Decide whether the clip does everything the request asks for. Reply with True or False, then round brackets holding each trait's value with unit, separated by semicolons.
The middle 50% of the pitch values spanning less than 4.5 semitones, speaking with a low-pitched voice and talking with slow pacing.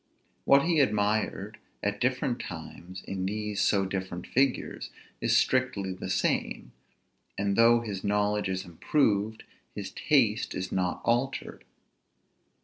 True (3.7 semitones; 105 Hz; 125 wpm)